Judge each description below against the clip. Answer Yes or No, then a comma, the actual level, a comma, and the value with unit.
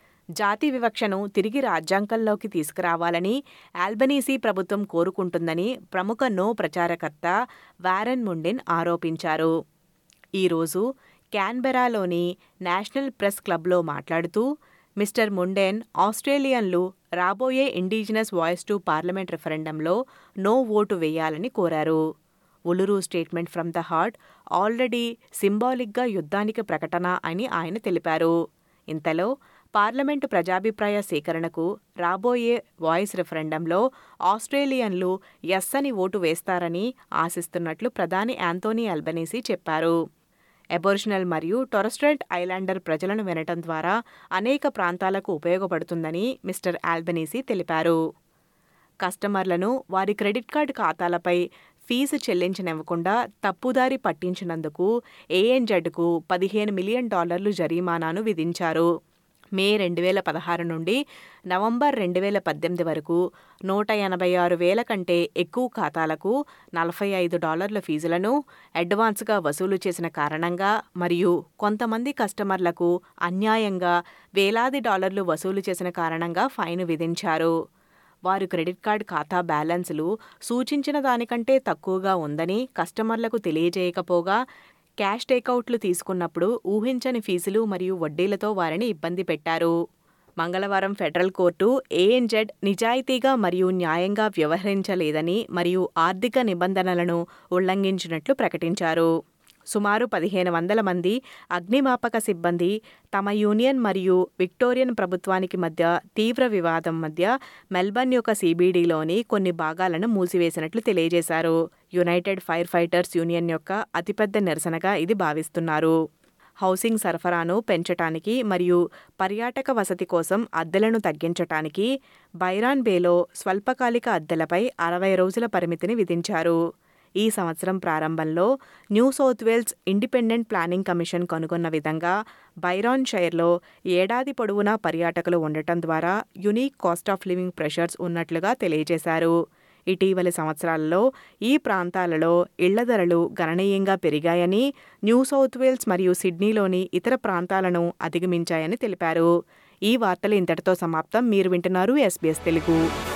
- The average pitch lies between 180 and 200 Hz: Yes, medium, 185 Hz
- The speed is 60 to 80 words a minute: No, average, 100 wpm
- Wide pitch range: No, average, 4.2 semitones